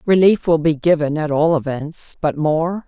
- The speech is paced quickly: No, average, 190 wpm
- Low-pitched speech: No, medium, 160 Hz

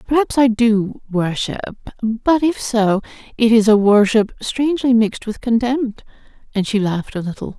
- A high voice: Yes, high, 225 Hz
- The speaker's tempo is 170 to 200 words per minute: No, average, 160 wpm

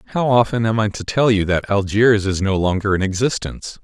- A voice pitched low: Yes, low, 105 Hz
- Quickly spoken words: Yes, fast, 220 wpm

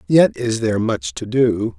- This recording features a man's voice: Yes, male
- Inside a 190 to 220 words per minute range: Yes, average, 200 wpm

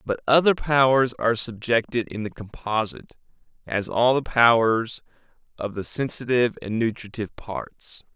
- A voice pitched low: Yes, low, 115 Hz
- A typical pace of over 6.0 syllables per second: No, 4.8 syllables/s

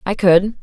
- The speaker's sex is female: Yes, female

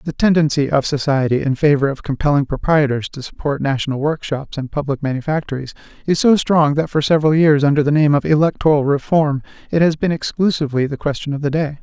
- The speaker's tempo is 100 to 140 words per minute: No, average, 195 wpm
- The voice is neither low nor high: Yes, medium, 145 Hz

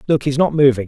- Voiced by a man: Yes, male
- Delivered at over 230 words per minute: Yes, fast, 275 wpm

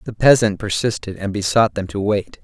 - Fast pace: No, average, 195 wpm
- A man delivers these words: Yes, male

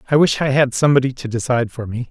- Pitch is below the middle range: Yes, low, 130 Hz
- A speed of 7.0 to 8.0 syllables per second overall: Yes, 7.4 syllables/s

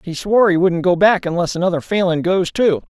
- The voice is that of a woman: No, male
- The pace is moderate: No, fast, 225 wpm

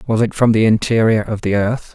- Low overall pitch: Yes, low, 110 Hz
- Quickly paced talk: Yes, fast, 245 wpm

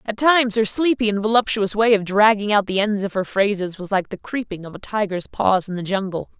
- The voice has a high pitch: Yes, high, 205 Hz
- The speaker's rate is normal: No, fast, 245 wpm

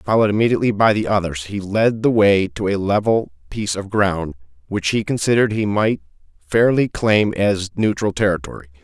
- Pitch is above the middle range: No, low, 100 Hz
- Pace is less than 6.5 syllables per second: Yes, 5.5 syllables/s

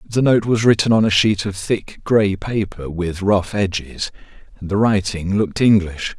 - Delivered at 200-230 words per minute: No, average, 175 wpm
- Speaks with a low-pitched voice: Yes, low, 100 Hz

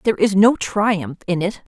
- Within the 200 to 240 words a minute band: Yes, fast, 205 wpm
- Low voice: No, high, 195 Hz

